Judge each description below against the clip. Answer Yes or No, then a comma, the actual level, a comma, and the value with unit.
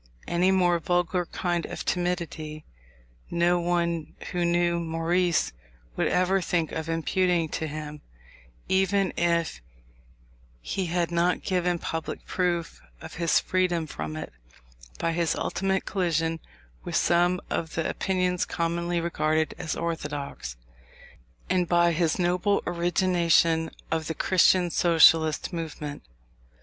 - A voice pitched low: No, medium, 170 Hz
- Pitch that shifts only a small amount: Yes, narrow, 1.6 semitones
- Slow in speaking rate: Yes, slow, 120 wpm